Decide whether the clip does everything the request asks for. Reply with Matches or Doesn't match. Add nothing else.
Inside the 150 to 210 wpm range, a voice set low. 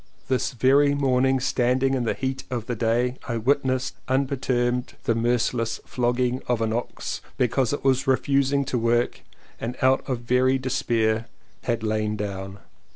Matches